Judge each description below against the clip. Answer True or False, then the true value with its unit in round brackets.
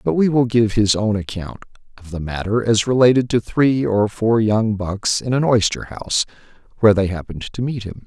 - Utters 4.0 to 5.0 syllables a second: False (5.2 syllables/s)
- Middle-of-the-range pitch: False (110 Hz)